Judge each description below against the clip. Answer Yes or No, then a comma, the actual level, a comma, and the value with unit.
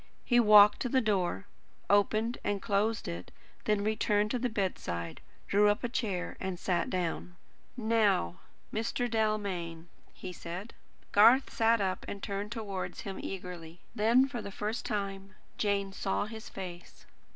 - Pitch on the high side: Yes, high, 205 Hz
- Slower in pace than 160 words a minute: Yes, average, 150 wpm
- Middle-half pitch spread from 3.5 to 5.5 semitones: No, average, 2.9 semitones